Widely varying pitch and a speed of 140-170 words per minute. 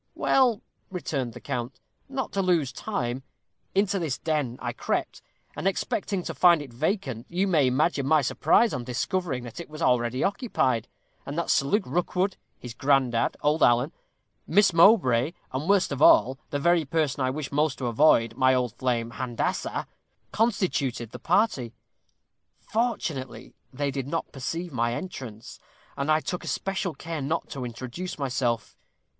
Yes: wide, 6.0 semitones; average, 160 wpm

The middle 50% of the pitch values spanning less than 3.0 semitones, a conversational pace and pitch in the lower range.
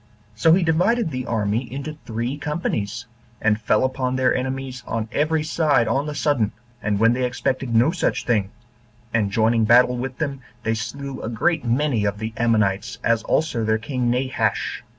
No: average, 3.9 semitones; average, 175 wpm; low, 125 Hz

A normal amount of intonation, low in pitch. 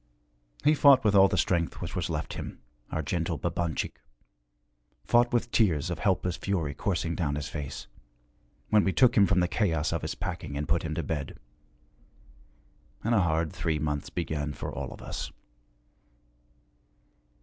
Yes: average, 4.1 semitones; very low, 85 Hz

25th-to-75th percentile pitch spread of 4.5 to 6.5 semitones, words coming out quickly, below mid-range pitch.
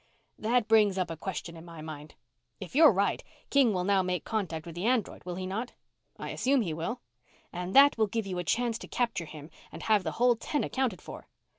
No: average, 5.2 semitones; fast, 225 wpm; high, 195 Hz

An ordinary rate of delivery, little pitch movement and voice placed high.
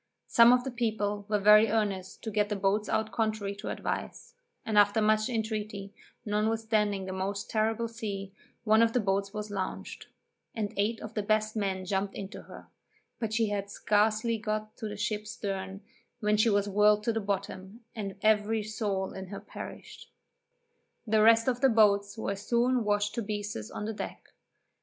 Yes: average, 180 wpm; narrow, 1.7 semitones; high, 210 Hz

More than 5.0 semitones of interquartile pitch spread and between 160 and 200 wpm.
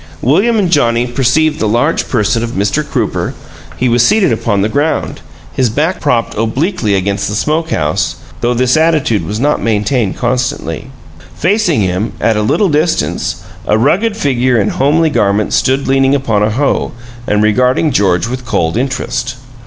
Yes: wide, 5.6 semitones; average, 170 wpm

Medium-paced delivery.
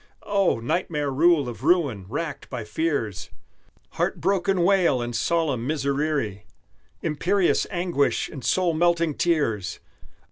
No: slow, 110 wpm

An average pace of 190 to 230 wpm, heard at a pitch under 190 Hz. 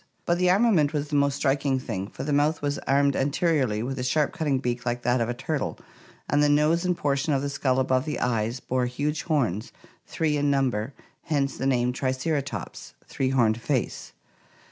Yes: average, 195 wpm; medium, 140 Hz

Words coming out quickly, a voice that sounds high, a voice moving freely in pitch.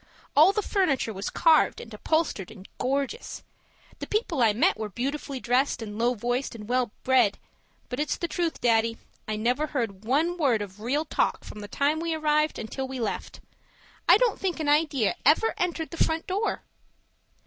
No: average, 180 wpm; very high, 265 Hz; wide, 5.9 semitones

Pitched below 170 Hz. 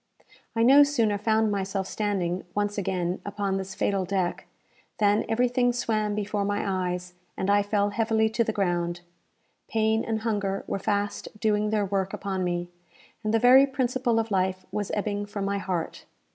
No: high, 205 Hz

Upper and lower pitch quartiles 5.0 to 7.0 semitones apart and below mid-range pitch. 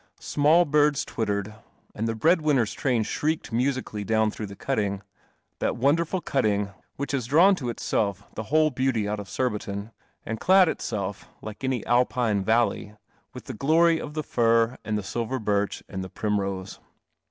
Yes: average, 5.3 semitones; low, 115 Hz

